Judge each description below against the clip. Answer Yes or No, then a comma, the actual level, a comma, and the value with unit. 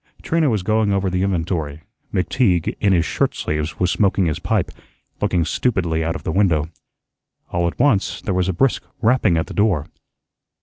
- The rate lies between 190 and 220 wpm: No, average, 180 wpm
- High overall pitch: No, very low, 90 Hz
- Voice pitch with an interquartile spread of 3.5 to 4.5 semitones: Yes, average, 4.0 semitones